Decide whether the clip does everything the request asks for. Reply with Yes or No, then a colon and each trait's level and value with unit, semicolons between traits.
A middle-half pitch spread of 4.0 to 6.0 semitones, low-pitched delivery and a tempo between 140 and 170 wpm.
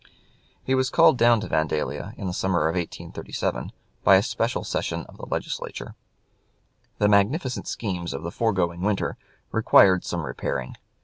Yes: average, 4.7 semitones; very low, 95 Hz; average, 150 wpm